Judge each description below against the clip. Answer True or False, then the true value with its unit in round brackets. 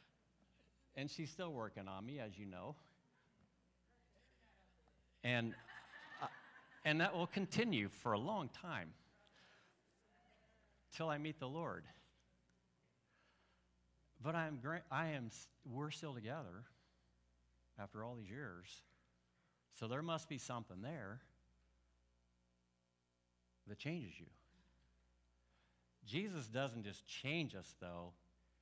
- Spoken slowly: True (105 wpm)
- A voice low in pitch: True (95 Hz)